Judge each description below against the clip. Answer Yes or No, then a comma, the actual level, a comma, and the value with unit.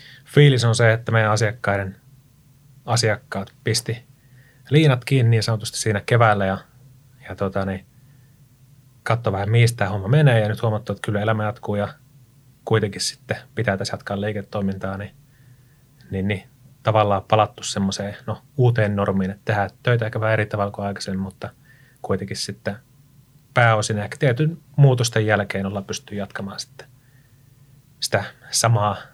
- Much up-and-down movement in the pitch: No, average, 4.3 semitones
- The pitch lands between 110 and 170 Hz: Yes, low, 115 Hz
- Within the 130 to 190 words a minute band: Yes, average, 140 wpm